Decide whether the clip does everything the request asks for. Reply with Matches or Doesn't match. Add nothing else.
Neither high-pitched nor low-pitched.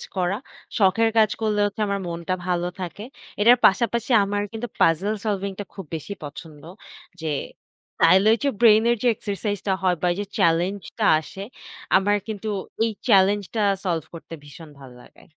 Doesn't match